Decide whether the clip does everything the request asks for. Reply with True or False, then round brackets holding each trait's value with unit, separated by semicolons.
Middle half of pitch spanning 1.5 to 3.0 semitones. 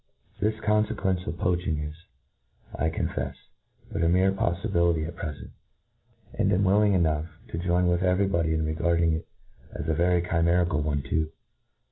True (2.4 semitones)